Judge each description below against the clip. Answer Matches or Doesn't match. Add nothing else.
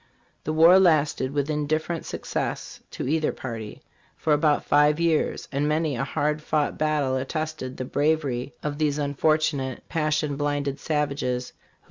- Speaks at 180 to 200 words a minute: Doesn't match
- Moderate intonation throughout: Doesn't match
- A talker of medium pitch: Matches